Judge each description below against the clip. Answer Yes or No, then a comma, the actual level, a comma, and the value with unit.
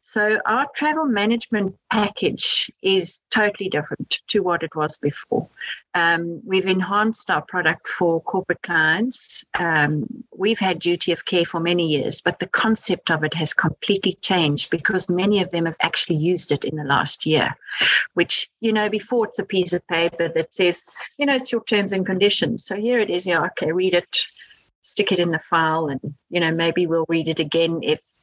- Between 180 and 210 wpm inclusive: Yes, average, 195 wpm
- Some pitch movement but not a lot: Yes, average, 3.9 semitones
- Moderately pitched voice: Yes, medium, 180 Hz